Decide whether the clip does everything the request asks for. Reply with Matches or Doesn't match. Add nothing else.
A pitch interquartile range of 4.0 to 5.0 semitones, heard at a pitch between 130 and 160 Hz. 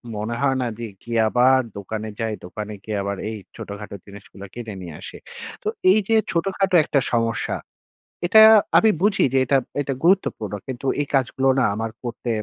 Doesn't match